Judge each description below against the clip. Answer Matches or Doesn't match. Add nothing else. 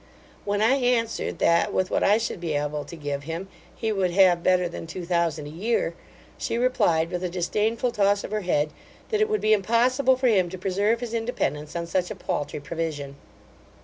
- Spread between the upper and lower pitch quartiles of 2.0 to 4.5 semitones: Doesn't match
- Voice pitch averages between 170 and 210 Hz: Matches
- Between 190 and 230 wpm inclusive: Matches